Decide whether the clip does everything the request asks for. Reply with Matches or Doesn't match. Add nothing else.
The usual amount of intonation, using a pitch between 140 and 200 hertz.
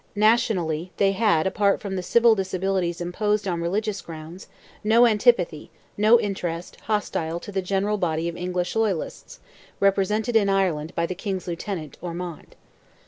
Matches